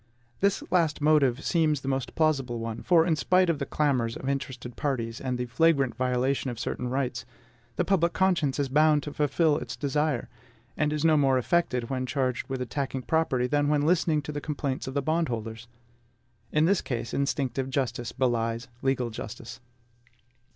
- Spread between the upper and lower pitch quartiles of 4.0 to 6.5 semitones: No, average, 3.5 semitones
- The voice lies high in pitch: No, low, 135 Hz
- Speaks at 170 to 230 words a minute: Yes, average, 175 wpm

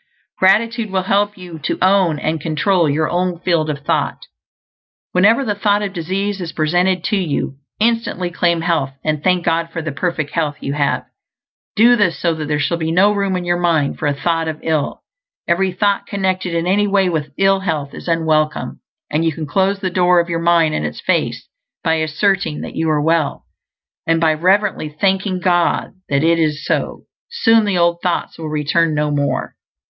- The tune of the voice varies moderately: Yes, average, 3.4 semitones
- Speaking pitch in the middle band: Yes, medium, 170 Hz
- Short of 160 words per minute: No, average, 195 wpm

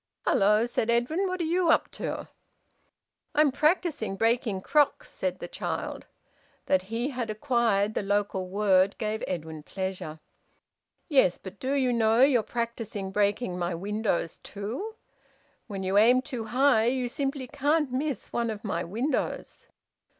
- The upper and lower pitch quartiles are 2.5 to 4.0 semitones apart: No, average, 5.0 semitones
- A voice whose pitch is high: Yes, high, 225 Hz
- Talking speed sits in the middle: Yes, average, 145 wpm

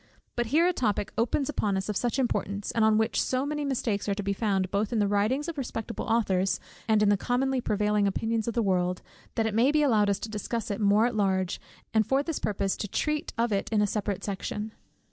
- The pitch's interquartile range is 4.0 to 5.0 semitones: No, average, 3.2 semitones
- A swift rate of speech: Yes, fast, 240 wpm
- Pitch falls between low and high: No, high, 215 Hz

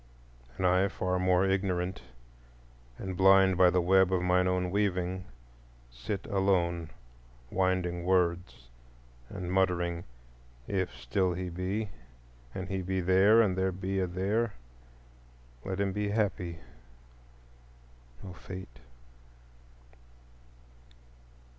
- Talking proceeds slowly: Yes, slow, 110 wpm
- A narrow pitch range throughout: Yes, narrow, 1.3 semitones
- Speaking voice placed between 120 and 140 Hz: No, very low, 95 Hz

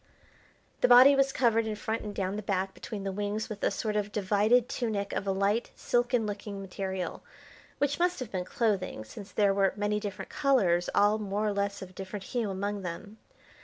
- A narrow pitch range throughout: Yes, narrow, 2.3 semitones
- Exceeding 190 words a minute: Yes, average, 200 wpm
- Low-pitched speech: No, high, 205 Hz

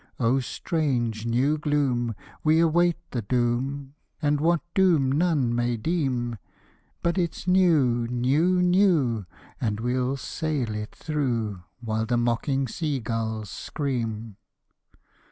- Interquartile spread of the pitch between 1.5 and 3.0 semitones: No, average, 4.9 semitones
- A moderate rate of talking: No, slow, 120 wpm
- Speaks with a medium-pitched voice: No, low, 130 Hz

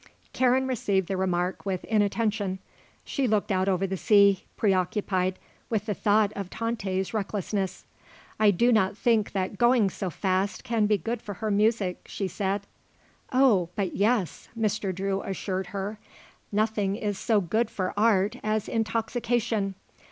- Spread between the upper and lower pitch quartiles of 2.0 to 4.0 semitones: Yes, narrow, 2.5 semitones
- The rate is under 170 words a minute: Yes, average, 150 wpm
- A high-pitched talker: Yes, high, 205 Hz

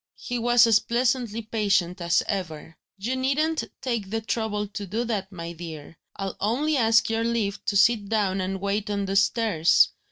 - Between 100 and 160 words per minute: No, average, 180 wpm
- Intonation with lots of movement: No, average, 3.3 semitones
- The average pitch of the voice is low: No, high, 210 Hz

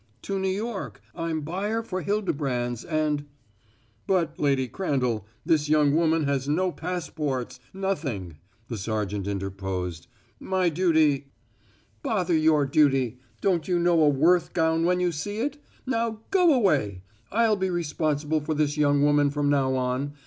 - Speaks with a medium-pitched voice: Yes, medium, 150 Hz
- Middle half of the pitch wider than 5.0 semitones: Yes, wide, 5.4 semitones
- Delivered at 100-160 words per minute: Yes, average, 150 wpm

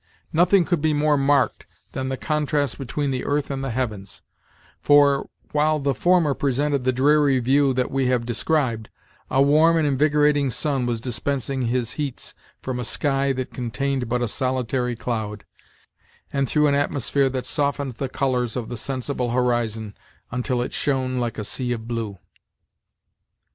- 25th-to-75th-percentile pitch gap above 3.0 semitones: No, average, 2.7 semitones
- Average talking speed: Yes, average, 165 wpm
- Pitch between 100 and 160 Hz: Yes, low, 135 Hz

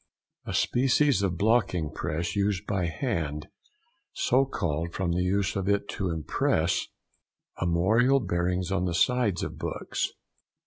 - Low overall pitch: Yes, very low, 95 Hz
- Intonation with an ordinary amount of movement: Yes, average, 4.2 semitones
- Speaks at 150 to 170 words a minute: No, slow, 135 wpm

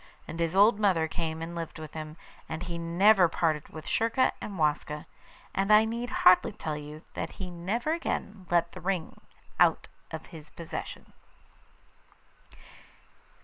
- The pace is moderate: Yes, average, 150 wpm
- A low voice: No, medium, 170 Hz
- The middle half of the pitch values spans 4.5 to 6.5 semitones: No, average, 3.9 semitones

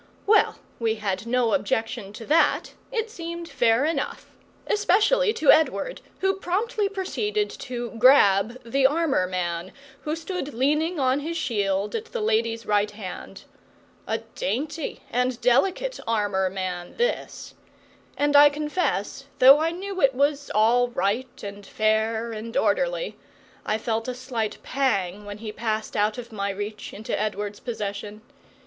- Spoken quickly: No, average, 145 wpm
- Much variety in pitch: Yes, wide, 7.2 semitones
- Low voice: No, high, 245 Hz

